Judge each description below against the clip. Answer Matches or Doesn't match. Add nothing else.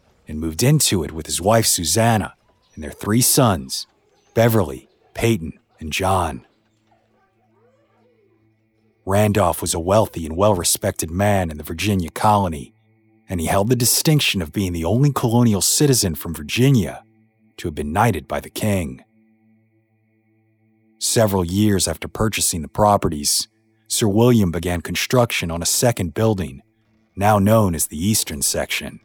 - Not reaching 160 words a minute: Matches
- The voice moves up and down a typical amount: Matches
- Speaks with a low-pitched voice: Matches